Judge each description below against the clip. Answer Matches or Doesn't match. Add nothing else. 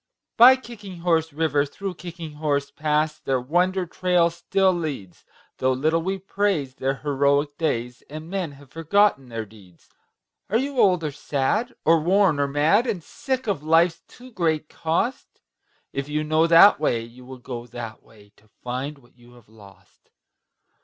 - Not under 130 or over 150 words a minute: Doesn't match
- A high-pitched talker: Doesn't match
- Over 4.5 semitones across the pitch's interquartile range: Matches